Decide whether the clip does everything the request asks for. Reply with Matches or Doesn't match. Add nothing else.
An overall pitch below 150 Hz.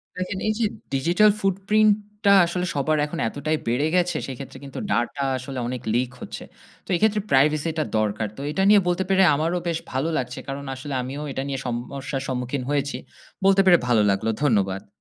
Matches